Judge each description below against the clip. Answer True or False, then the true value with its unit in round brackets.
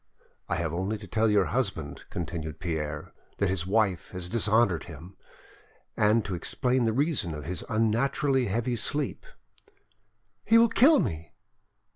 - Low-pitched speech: True (100 Hz)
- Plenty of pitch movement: True (5.9 semitones)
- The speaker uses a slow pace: False (145 wpm)